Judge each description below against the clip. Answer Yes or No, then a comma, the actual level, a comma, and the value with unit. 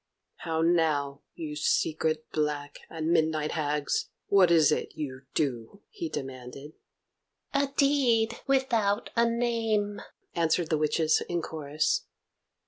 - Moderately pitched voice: Yes, medium, 160 Hz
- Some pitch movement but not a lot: No, wide, 6.5 semitones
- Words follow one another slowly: Yes, slow, 120 wpm